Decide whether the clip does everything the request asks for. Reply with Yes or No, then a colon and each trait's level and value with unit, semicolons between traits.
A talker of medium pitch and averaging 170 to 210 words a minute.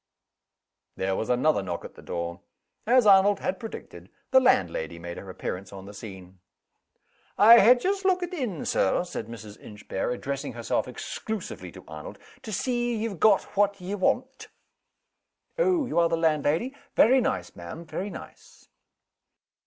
No: medium, 180 Hz; average, 155 wpm